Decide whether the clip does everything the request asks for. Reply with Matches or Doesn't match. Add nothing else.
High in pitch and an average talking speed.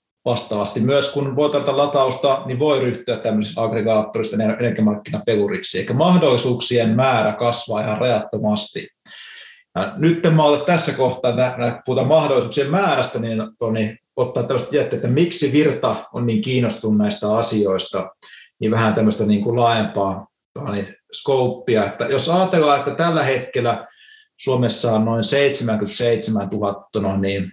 Doesn't match